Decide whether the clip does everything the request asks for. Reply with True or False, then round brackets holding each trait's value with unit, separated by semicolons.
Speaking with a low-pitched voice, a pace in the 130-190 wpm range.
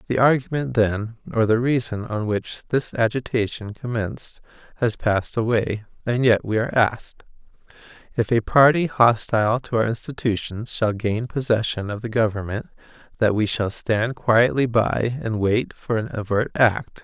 True (115 Hz; 155 wpm)